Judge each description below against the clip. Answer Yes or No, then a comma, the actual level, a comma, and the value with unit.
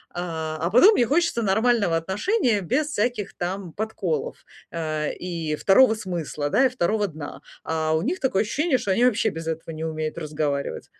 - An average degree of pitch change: No, wide, 6.6 semitones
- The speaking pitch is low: No, high, 190 Hz